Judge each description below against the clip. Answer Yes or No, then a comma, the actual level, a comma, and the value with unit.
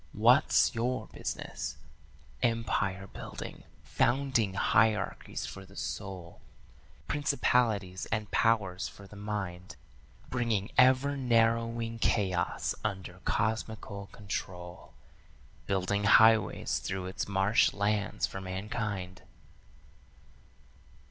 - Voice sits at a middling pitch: No, low, 105 Hz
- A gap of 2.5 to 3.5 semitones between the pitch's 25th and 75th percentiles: Yes, average, 3.1 semitones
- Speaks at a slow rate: Yes, slow, 90 wpm